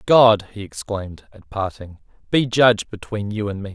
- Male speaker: Yes, male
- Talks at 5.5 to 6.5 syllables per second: No, 4.9 syllables/s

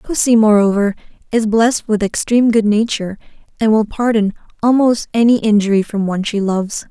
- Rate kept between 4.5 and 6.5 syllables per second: Yes, 5.8 syllables/s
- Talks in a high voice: Yes, high, 215 Hz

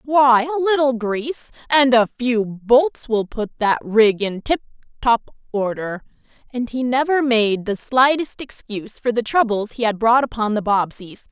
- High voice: Yes, high, 240 Hz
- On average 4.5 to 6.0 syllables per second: No, 4.3 syllables/s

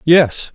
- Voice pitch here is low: No, medium, 155 Hz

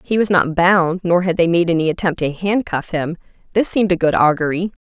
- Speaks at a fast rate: Yes, fast, 225 wpm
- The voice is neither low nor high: Yes, medium, 175 Hz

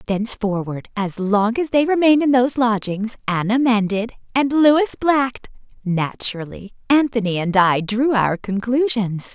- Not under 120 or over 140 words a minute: Yes, slow, 135 wpm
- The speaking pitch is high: Yes, high, 230 Hz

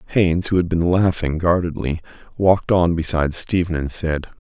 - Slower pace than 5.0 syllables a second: No, 5.4 syllables/s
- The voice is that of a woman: No, male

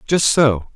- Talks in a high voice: No, low, 130 Hz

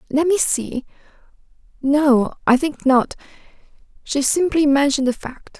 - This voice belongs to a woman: Yes, female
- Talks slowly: Yes, slow, 95 wpm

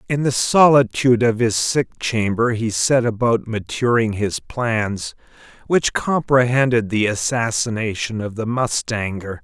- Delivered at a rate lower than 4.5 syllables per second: Yes, 4.1 syllables/s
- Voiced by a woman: No, male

